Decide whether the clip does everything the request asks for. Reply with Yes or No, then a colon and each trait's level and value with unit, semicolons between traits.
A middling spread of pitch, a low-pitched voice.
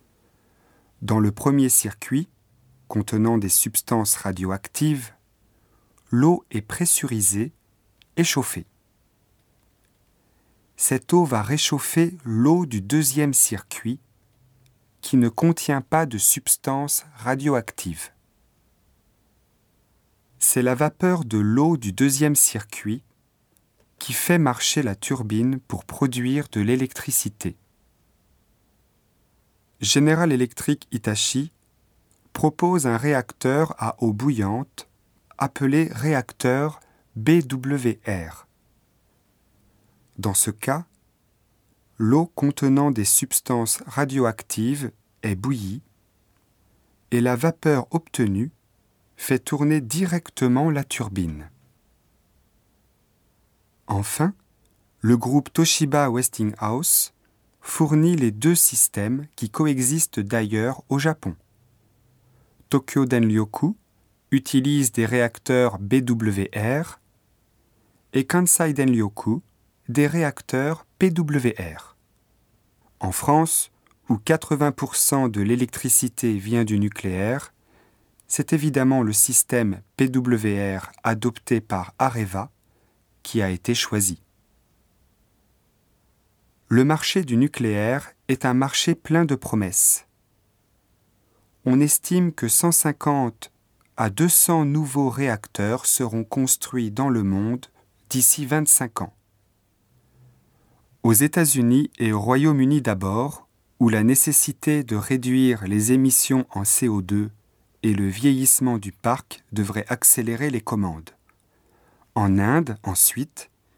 Yes: average, 4.9 semitones; low, 120 Hz